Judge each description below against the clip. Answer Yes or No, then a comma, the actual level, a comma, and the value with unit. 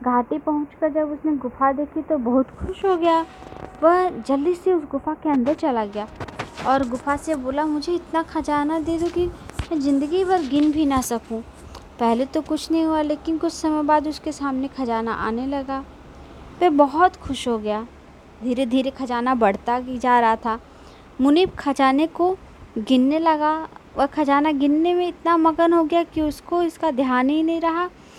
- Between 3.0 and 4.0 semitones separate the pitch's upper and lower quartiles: Yes, average, 3.7 semitones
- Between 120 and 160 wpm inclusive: No, average, 180 wpm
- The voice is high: Yes, very high, 300 Hz